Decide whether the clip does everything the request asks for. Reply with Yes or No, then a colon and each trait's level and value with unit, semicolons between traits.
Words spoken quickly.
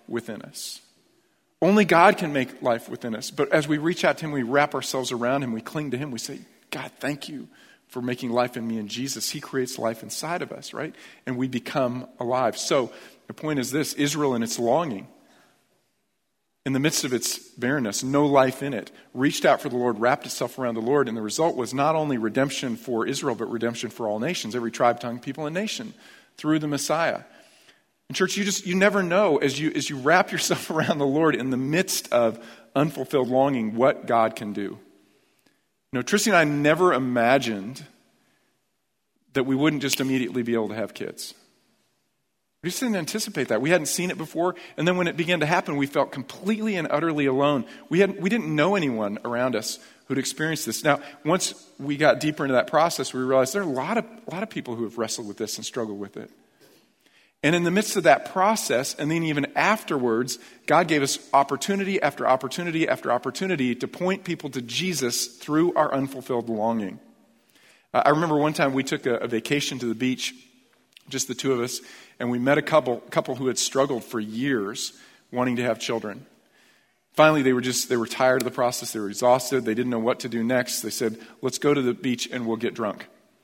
Yes: fast, 215 wpm